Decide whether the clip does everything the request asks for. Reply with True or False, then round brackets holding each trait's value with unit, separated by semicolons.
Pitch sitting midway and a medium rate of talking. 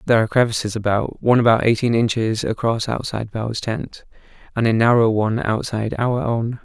False (115 Hz; 170 wpm)